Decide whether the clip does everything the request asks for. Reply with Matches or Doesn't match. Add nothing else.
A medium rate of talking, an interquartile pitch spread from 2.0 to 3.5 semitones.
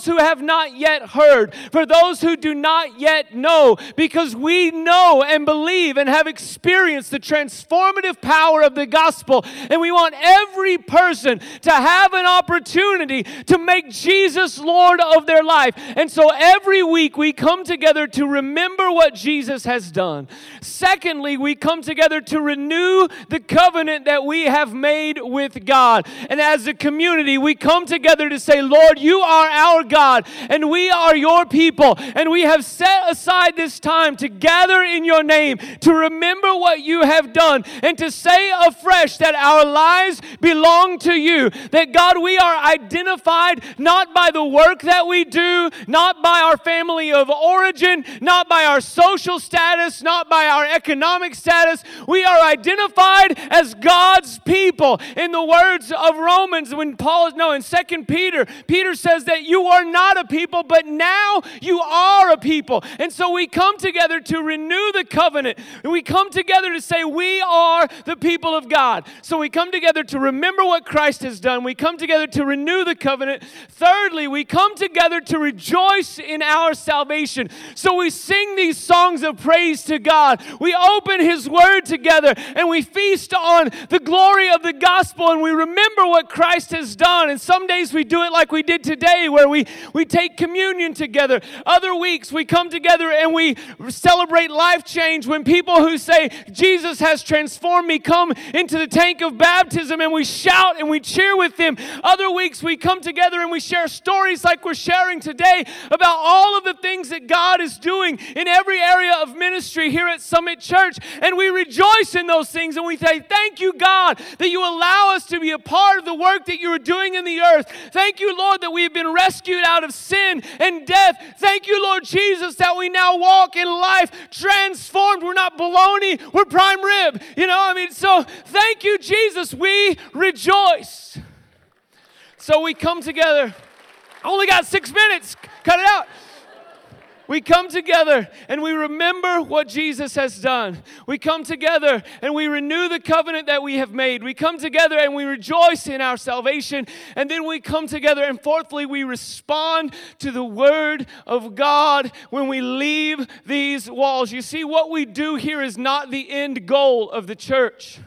Matches